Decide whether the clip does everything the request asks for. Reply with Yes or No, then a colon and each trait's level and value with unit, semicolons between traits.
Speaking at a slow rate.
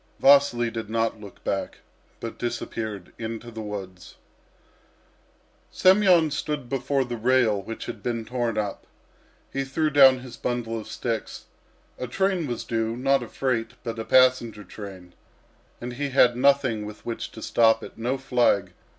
No: average, 155 wpm